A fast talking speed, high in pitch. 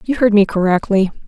No: average, 190 wpm; high, 205 Hz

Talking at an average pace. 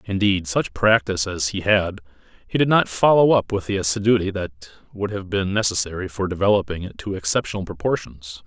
Yes: average, 175 wpm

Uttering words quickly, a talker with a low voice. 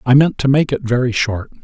Yes: fast, 255 wpm; low, 130 Hz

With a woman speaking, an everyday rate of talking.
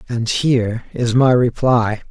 No: male; average, 145 wpm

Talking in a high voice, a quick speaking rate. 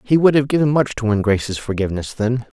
No: low, 120 Hz; fast, 230 wpm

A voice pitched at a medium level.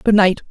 No: high, 200 Hz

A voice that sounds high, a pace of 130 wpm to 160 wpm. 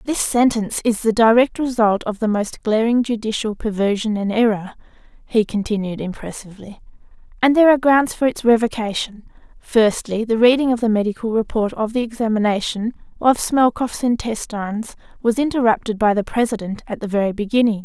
Yes: high, 225 Hz; average, 155 wpm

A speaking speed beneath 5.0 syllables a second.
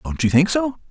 No: 5.5 syllables/s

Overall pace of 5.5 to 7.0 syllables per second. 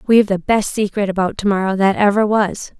Yes: 5.7 syllables/s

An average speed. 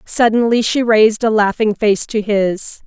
Yes: average, 165 wpm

